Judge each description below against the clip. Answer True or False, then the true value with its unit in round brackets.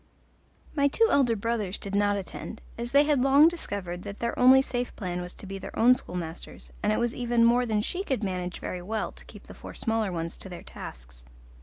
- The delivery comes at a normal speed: False (220 wpm)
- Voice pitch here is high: True (220 Hz)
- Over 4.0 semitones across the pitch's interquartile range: True (5.2 semitones)